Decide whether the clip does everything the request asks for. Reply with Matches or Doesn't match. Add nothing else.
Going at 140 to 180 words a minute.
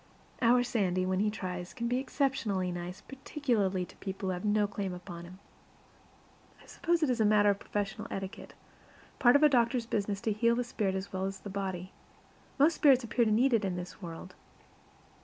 Doesn't match